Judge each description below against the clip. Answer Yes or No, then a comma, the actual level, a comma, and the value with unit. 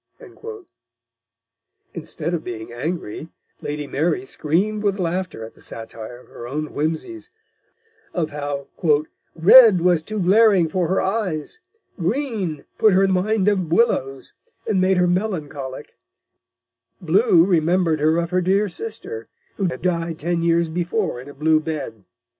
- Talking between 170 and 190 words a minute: No, average, 140 wpm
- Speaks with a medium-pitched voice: Yes, medium, 170 Hz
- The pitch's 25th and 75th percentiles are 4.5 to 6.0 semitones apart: No, average, 4.0 semitones